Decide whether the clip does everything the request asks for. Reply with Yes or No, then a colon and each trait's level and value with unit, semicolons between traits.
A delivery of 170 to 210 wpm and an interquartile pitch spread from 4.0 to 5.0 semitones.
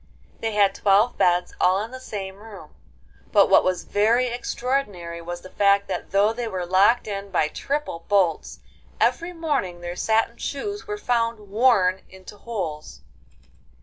No: average, 155 wpm; average, 4.3 semitones